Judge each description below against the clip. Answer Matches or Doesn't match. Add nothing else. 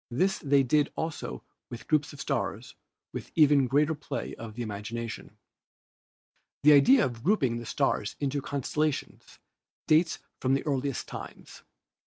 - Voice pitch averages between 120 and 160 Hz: Matches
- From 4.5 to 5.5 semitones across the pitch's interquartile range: Doesn't match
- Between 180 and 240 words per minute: Doesn't match